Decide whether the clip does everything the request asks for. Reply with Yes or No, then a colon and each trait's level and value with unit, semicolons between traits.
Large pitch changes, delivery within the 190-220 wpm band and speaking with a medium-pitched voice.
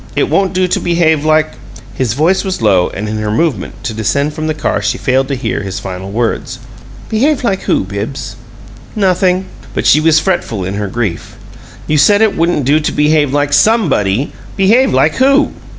Yes: wide, 8.4 semitones; average, 195 wpm; medium, 150 Hz